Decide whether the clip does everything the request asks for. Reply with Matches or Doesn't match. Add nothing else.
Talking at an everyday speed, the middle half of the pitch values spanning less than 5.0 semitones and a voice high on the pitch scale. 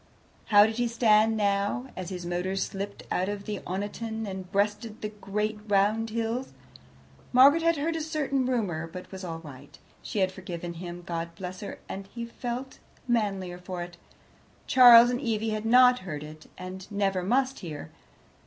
Matches